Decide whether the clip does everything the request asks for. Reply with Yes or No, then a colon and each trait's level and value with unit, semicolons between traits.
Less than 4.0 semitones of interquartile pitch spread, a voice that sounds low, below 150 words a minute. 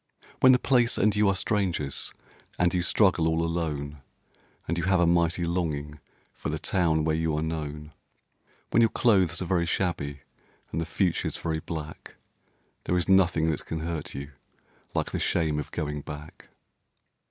No: average, 3.0 semitones; very low, 85 Hz; average, 170 wpm